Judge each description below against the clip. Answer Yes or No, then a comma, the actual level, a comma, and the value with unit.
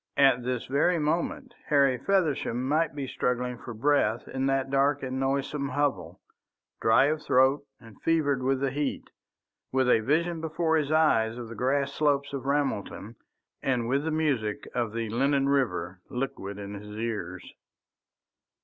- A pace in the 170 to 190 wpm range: No, average, 160 wpm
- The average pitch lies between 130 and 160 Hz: Yes, low, 135 Hz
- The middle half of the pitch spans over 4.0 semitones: No, average, 3.4 semitones